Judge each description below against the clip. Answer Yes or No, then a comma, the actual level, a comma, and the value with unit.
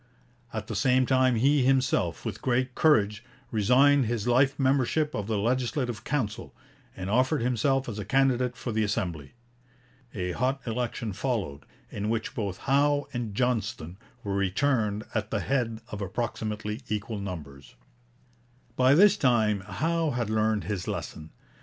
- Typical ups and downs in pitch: Yes, average, 4.1 semitones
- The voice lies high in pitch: No, low, 115 Hz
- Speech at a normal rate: Yes, average, 145 wpm